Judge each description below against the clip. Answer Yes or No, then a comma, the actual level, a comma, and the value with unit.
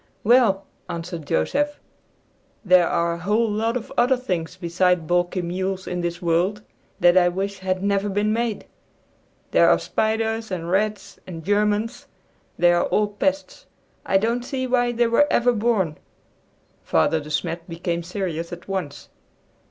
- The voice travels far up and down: No, average, 4.3 semitones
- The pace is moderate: Yes, average, 150 wpm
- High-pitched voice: Yes, high, 195 Hz